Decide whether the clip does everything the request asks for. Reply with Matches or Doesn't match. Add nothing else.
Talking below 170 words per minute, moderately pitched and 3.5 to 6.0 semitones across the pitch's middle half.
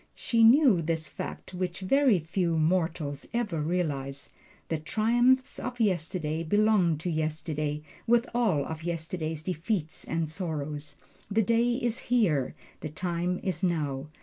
Matches